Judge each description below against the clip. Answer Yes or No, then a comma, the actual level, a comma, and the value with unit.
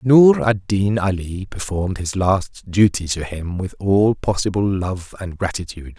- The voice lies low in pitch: Yes, very low, 95 Hz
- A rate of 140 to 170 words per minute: Yes, average, 160 wpm